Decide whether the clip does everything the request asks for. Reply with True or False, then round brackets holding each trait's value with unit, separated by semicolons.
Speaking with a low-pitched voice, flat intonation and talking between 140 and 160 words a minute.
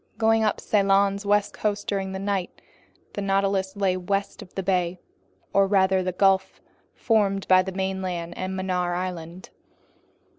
False (190 Hz; 1.3 semitones; 150 wpm)